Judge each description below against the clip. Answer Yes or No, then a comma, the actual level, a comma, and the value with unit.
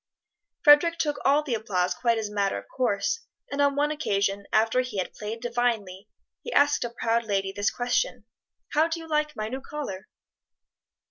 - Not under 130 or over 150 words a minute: No, average, 185 wpm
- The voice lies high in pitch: Yes, high, 240 Hz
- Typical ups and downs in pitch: No, wide, 6.2 semitones